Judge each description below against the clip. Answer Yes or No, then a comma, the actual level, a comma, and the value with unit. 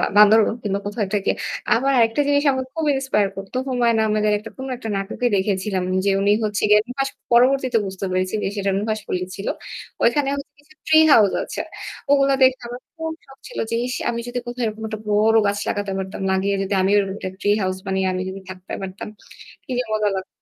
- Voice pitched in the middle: No, high, 215 Hz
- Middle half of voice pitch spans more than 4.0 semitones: Yes, average, 4.4 semitones